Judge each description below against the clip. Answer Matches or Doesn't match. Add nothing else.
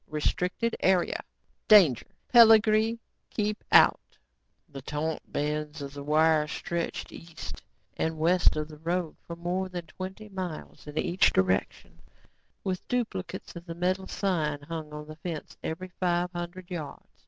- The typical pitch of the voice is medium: Matches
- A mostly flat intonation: Doesn't match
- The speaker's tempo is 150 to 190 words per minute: Doesn't match